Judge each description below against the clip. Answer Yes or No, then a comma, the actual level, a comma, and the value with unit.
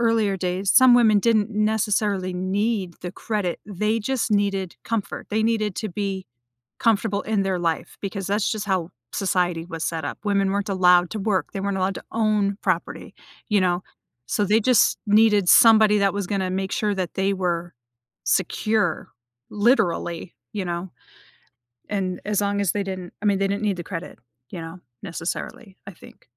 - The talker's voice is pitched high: Yes, high, 200 Hz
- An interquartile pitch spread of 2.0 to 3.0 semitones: Yes, narrow, 2.4 semitones